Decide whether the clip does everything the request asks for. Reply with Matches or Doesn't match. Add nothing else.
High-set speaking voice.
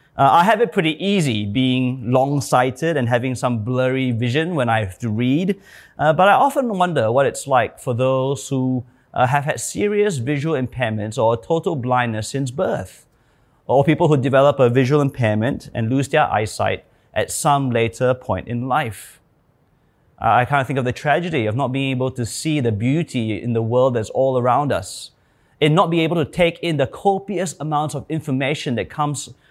Doesn't match